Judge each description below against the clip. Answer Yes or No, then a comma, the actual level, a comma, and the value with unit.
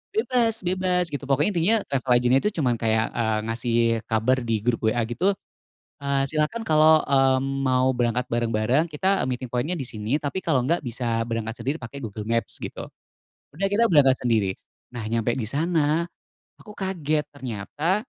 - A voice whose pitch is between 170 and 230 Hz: No, low, 130 Hz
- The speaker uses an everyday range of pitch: No, wide, 5.7 semitones